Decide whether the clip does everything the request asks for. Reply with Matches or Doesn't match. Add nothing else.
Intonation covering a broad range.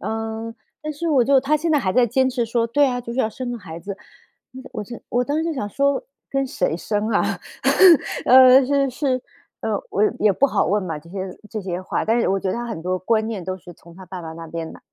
Matches